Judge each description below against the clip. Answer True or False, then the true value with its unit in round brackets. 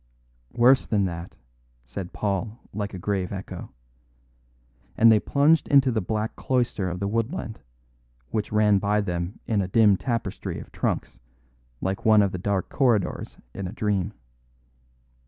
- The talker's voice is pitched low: True (105 Hz)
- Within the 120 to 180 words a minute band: True (150 wpm)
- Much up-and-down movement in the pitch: False (3.0 semitones)